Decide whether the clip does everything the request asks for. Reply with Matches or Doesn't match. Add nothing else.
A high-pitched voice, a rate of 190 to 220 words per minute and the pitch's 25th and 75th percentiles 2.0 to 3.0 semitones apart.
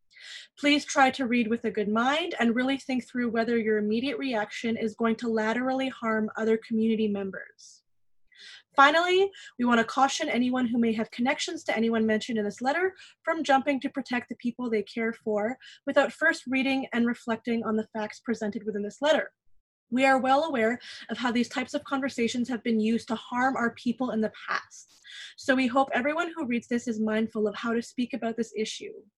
Doesn't match